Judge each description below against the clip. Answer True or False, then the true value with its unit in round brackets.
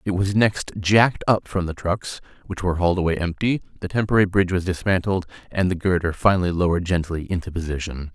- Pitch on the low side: True (90 Hz)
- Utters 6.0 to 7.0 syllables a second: True (6.4 syllables/s)